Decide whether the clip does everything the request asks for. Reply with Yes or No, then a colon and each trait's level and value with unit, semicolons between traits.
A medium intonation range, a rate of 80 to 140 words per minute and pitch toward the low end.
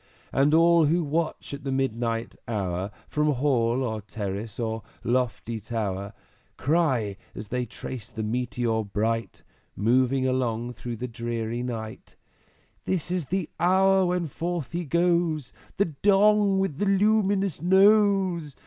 No: wide, 7.2 semitones; slow, 135 wpm; low, 130 Hz